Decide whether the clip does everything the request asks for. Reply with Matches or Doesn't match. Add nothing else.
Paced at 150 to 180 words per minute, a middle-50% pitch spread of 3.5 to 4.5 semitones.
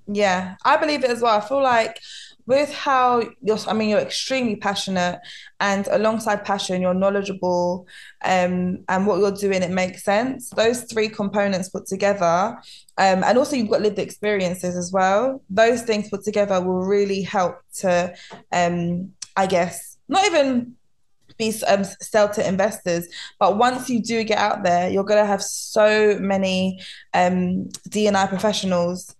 Doesn't match